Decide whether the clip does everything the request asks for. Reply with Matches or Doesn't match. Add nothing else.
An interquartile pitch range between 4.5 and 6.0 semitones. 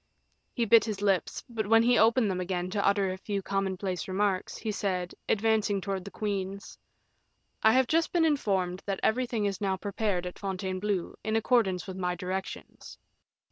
Doesn't match